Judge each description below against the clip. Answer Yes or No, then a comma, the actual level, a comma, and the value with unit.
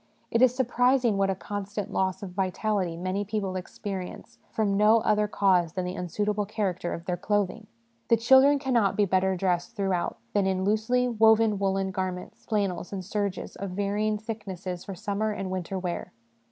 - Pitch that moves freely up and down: No, narrow, 2.5 semitones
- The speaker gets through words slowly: No, average, 170 wpm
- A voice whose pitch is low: No, high, 200 Hz